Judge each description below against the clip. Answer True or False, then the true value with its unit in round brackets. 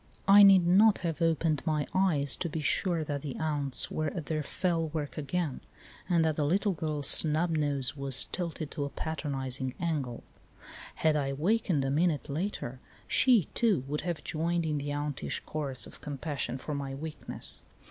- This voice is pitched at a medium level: True (155 Hz)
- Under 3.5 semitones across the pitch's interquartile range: True (3.1 semitones)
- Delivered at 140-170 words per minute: False (180 wpm)